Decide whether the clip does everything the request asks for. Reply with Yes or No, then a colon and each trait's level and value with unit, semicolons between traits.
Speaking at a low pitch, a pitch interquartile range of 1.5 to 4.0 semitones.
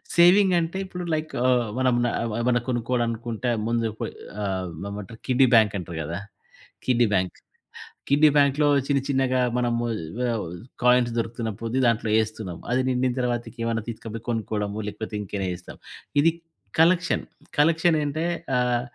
Yes: low, 120 Hz; average, 3.6 semitones